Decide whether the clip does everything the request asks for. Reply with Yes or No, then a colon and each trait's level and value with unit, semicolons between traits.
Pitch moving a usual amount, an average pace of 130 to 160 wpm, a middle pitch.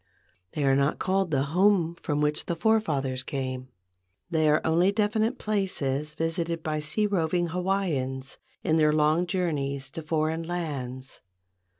Yes: average, 4.3 semitones; average, 140 wpm; medium, 160 Hz